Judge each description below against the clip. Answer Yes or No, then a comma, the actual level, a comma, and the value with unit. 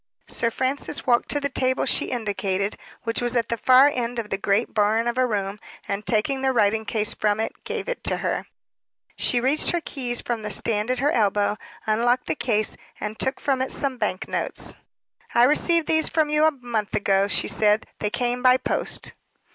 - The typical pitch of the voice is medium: No, high, 240 Hz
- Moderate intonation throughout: Yes, average, 3.6 semitones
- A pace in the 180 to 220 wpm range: Yes, fast, 205 wpm